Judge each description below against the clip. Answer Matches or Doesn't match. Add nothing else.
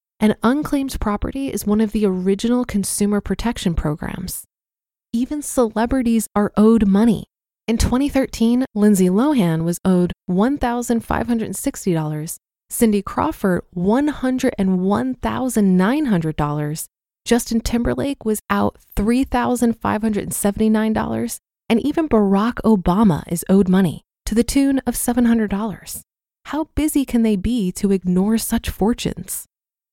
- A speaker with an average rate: Doesn't match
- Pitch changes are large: Doesn't match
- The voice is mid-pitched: Doesn't match